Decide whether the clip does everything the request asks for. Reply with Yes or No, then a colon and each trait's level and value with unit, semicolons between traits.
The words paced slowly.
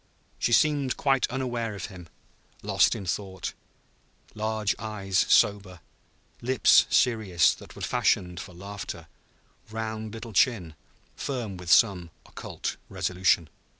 Yes: slow, 115 wpm